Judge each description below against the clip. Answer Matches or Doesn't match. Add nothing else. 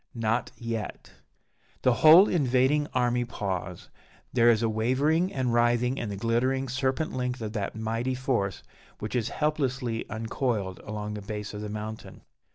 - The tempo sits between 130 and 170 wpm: Matches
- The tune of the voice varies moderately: Matches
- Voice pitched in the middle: Doesn't match